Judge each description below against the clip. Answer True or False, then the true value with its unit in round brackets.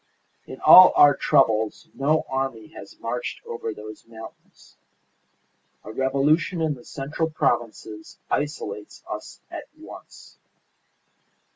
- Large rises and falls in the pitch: False (4.9 semitones)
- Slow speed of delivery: True (110 wpm)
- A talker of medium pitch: False (130 Hz)